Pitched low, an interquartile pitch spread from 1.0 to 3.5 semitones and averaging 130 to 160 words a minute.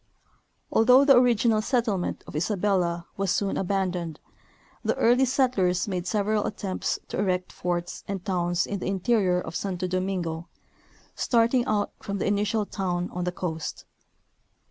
No: high, 195 Hz; average, 3.2 semitones; average, 145 wpm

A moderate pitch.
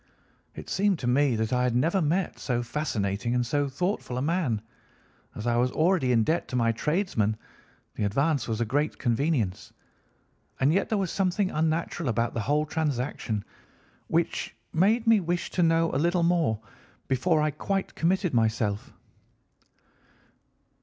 Yes: medium, 145 Hz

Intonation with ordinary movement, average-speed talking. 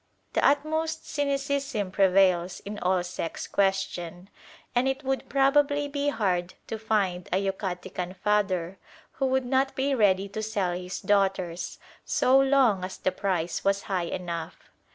No: wide, 6.7 semitones; average, 145 wpm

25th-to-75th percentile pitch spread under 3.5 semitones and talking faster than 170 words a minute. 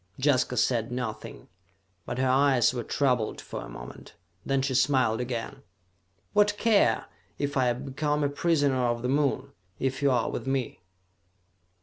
No: narrow, 2.5 semitones; average, 155 wpm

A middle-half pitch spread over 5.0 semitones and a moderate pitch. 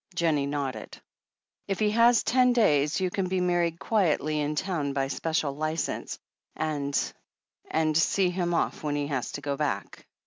No: average, 4.0 semitones; medium, 155 Hz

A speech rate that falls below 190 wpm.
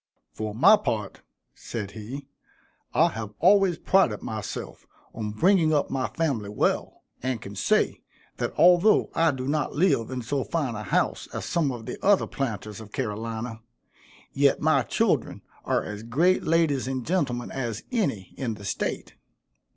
Yes: average, 160 wpm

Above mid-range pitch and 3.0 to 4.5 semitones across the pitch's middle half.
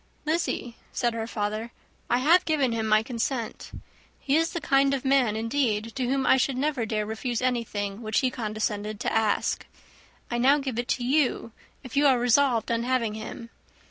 Yes: high, 240 Hz; average, 3.6 semitones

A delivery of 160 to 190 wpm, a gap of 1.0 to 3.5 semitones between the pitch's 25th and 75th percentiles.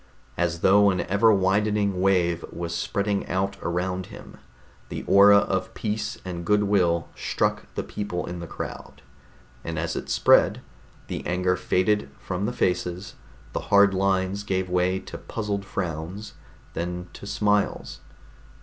No: average, 145 wpm; narrow, 2.4 semitones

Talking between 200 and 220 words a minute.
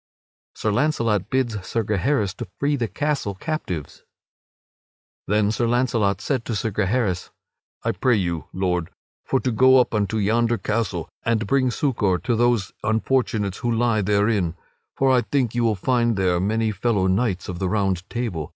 No: average, 170 wpm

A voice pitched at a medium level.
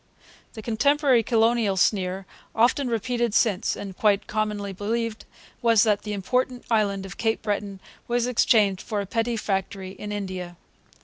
No: high, 215 Hz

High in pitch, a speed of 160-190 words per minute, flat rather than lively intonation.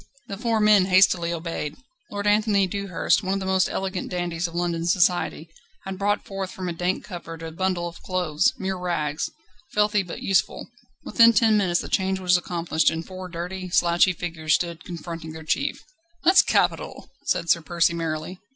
No: medium, 180 Hz; average, 180 wpm; narrow, 2.3 semitones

